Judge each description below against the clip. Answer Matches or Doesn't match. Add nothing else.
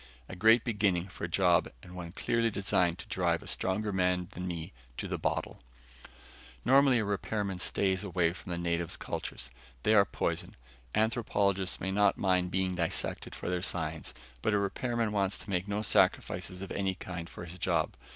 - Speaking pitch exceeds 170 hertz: Doesn't match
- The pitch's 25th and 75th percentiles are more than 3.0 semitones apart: Doesn't match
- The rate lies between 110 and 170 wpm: Doesn't match